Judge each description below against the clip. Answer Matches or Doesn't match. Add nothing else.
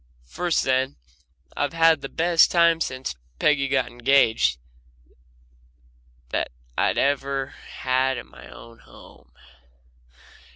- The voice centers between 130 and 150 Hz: Matches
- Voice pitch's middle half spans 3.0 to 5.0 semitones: Matches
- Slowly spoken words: Matches